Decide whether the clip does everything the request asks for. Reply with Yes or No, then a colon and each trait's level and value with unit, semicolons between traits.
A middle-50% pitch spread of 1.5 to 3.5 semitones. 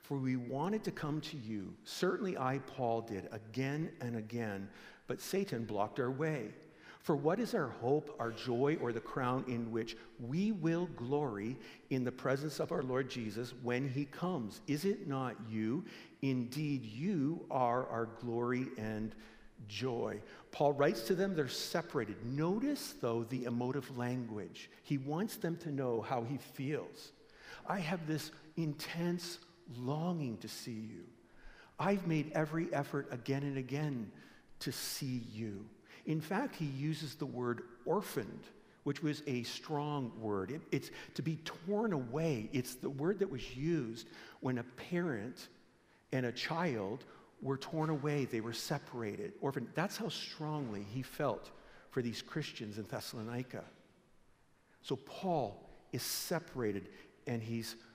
No: average, 5.0 semitones